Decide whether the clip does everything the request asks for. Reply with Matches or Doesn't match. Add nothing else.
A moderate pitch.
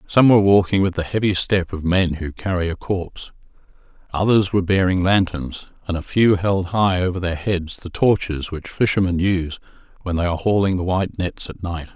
Doesn't match